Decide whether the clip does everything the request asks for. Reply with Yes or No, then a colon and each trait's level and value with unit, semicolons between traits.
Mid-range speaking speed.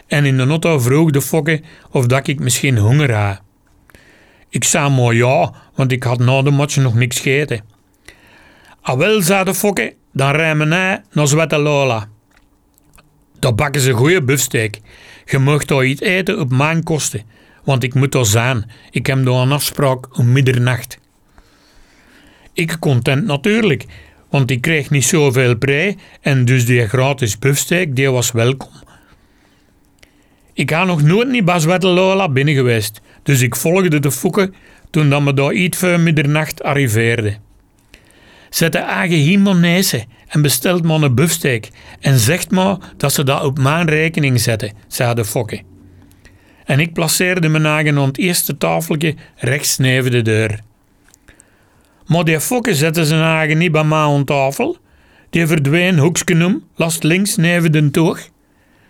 Yes: average, 155 wpm